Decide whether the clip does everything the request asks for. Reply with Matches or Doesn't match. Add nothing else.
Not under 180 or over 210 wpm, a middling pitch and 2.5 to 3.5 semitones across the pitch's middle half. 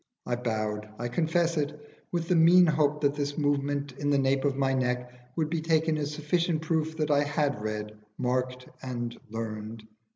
Doesn't match